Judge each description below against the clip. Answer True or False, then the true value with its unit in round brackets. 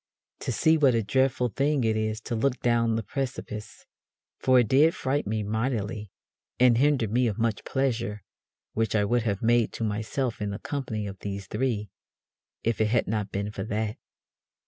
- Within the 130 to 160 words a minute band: False (185 wpm)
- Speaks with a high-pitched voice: False (115 Hz)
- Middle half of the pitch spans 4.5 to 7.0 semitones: False (3.2 semitones)